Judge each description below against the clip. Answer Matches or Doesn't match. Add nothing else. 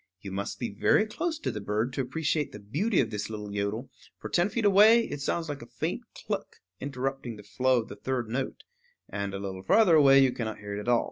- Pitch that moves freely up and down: Matches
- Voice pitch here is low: Matches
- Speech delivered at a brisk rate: Matches